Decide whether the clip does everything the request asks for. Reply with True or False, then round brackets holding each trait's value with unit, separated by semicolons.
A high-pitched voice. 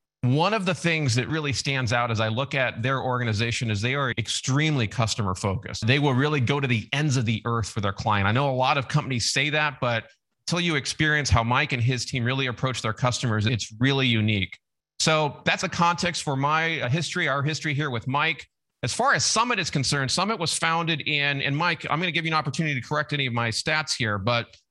False (135 Hz)